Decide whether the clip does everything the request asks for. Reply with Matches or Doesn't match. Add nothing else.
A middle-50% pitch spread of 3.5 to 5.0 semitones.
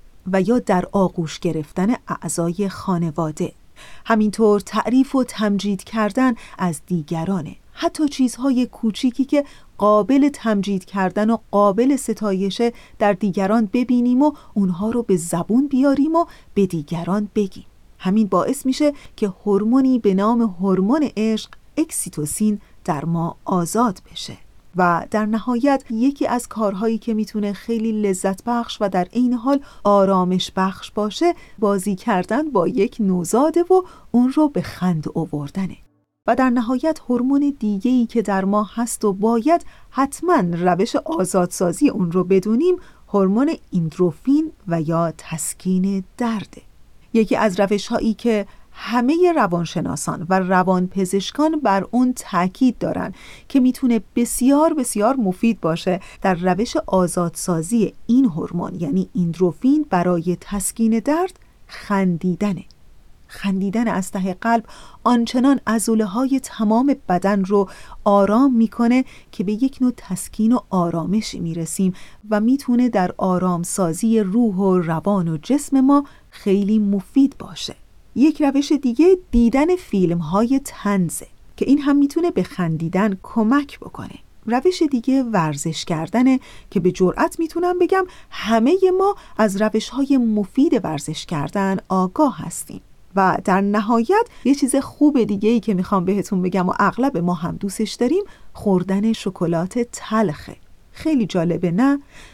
Doesn't match